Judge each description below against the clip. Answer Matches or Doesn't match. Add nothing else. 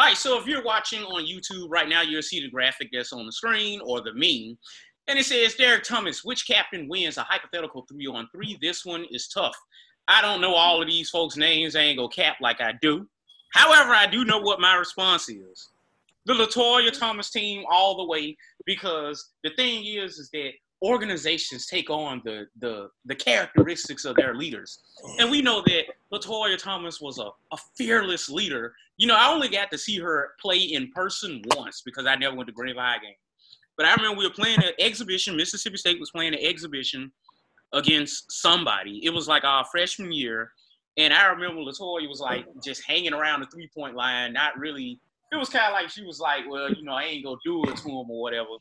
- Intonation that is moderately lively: Doesn't match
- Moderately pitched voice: Matches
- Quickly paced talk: Matches